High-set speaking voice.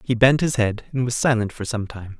No: low, 115 Hz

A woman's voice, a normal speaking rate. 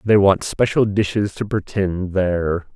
No: male; average, 155 wpm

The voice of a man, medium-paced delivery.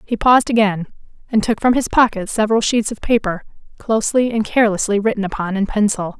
No: female; average, 185 wpm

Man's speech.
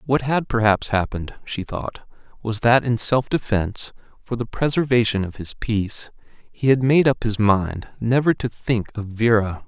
Yes: male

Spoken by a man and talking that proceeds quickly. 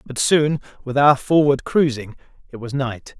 No: male; average, 170 wpm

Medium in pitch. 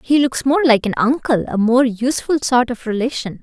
No: very high, 250 Hz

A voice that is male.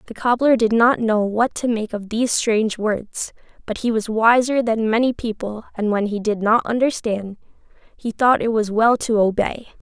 No: female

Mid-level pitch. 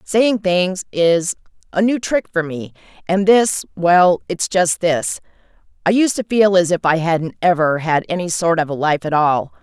Yes: medium, 175 Hz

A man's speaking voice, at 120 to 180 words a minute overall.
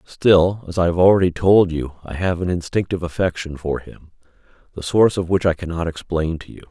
No: male; fast, 205 wpm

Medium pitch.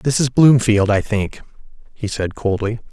No: low, 110 Hz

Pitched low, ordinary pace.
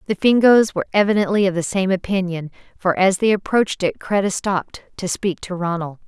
No: high, 190 Hz; average, 190 wpm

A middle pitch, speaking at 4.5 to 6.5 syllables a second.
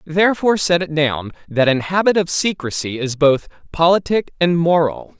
Yes: medium, 165 Hz; 5.0 syllables/s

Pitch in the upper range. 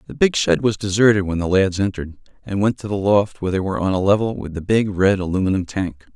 No: low, 100 Hz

